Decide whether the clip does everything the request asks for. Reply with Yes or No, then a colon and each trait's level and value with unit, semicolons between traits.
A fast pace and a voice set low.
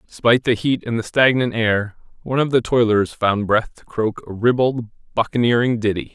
No: average, 185 wpm; low, 115 Hz